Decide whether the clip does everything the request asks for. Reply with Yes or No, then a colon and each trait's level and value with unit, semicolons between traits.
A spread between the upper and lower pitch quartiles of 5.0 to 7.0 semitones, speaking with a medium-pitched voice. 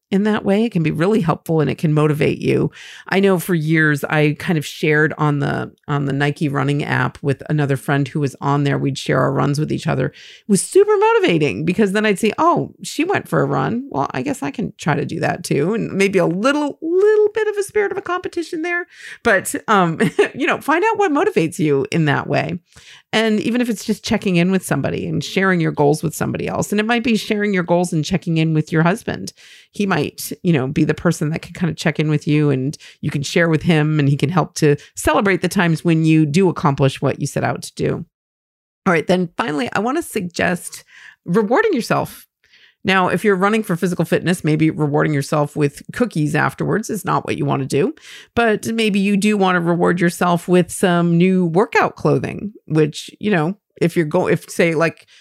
Yes: wide, 5.5 semitones; medium, 175 Hz